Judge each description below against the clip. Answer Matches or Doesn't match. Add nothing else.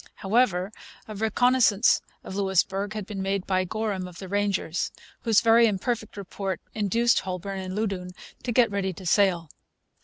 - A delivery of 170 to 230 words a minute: Doesn't match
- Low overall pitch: Doesn't match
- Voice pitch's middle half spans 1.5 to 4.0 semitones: Matches